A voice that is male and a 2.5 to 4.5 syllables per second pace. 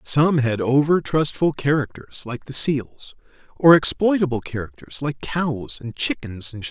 Yes: male; 4.4 syllables/s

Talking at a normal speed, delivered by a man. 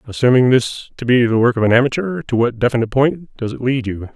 No: fast, 245 wpm; male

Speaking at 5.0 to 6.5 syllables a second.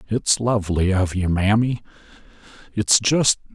No: 4.4 syllables/s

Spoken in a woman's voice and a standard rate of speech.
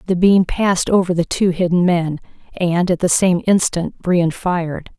Yes: female; average, 180 wpm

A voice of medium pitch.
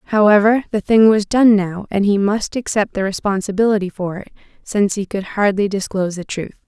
No: high, 205 Hz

